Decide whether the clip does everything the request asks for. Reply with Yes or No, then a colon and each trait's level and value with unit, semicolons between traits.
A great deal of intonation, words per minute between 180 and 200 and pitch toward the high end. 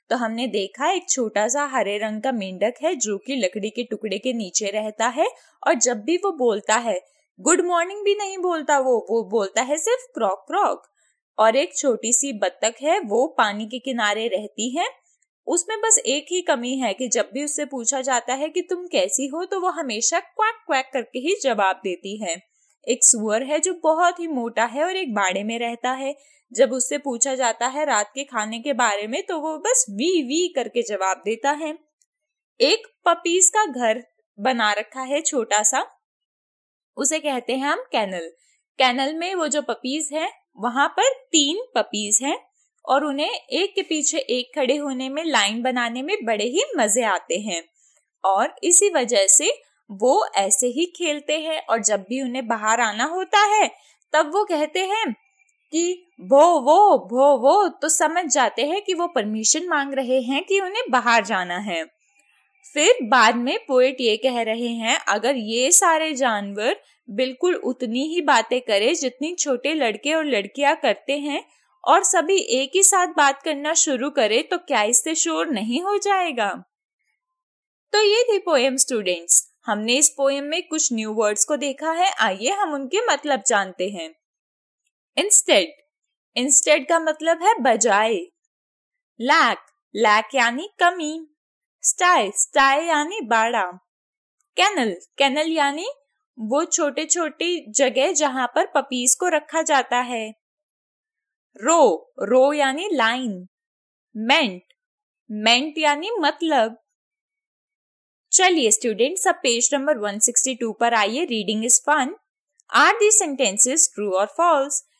No: wide, 6.3 semitones; average, 160 wpm; very high, 280 Hz